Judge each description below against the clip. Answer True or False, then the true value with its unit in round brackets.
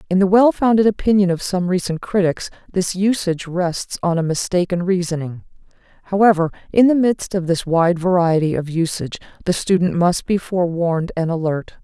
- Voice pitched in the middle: True (180 Hz)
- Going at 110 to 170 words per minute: True (165 wpm)